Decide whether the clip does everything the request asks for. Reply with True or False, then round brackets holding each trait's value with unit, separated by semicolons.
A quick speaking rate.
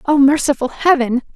False (135 wpm)